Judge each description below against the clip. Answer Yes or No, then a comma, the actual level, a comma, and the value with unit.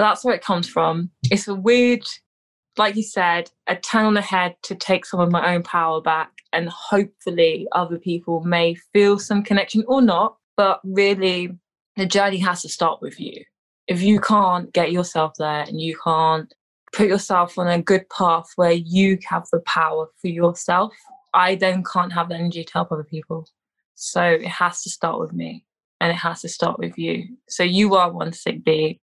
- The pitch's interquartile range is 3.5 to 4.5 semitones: No, average, 3.0 semitones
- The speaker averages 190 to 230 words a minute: Yes, average, 195 wpm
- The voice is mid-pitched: Yes, medium, 180 Hz